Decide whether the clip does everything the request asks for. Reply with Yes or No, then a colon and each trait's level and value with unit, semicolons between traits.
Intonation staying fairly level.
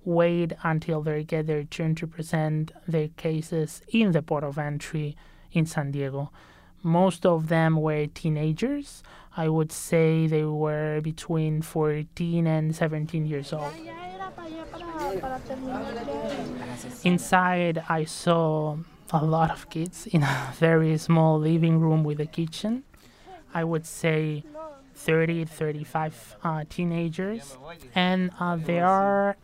Yes: narrow, 2.1 semitones